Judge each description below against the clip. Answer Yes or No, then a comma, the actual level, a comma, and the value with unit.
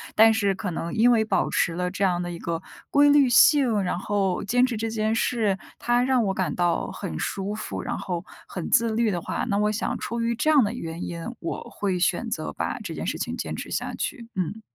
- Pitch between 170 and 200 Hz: No, high, 210 Hz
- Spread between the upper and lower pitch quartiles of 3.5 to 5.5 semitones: Yes, average, 4.5 semitones